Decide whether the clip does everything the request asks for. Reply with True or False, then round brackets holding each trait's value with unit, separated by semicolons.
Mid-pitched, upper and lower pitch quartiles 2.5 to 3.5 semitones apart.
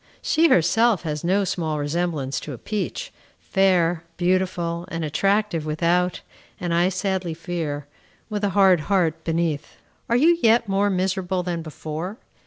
True (175 Hz; 3.1 semitones)